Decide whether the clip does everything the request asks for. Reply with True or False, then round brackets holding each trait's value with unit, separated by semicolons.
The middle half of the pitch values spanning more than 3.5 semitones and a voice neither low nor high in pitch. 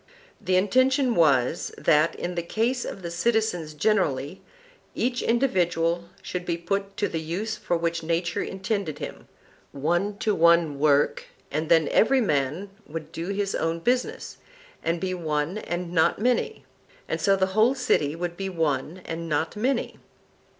True (4.0 semitones; 175 Hz)